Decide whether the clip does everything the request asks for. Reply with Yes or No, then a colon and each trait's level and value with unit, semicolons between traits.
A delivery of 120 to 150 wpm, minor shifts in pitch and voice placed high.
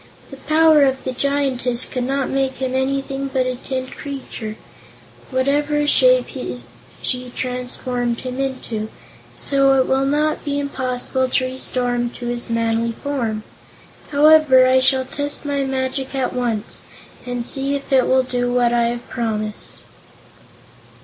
Yes: average, 145 wpm; narrow, 2.0 semitones; very high, 260 Hz